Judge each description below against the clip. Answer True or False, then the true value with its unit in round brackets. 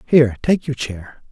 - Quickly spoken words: False (185 wpm)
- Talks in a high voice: False (130 Hz)